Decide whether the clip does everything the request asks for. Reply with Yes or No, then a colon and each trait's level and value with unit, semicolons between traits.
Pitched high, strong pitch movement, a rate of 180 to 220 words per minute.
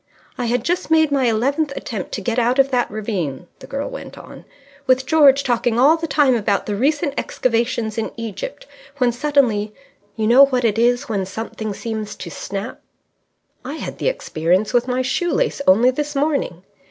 No: high, 245 Hz; average, 4.4 semitones; average, 190 wpm